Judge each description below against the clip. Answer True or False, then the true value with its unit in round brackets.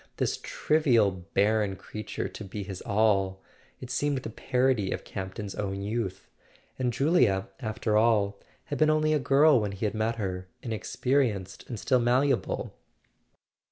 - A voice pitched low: True (110 Hz)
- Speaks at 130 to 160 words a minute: True (155 wpm)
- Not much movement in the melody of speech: False (4.6 semitones)